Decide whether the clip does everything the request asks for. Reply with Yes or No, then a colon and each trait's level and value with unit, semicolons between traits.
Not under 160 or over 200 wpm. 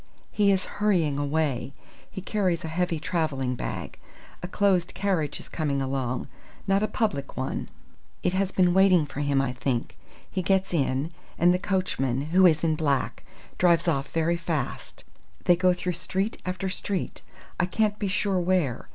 Yes: average, 170 wpm